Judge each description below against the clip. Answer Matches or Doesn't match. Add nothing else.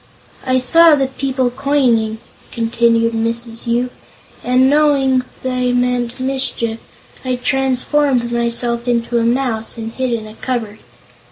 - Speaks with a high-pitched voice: Matches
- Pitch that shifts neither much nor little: Doesn't match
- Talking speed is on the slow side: Matches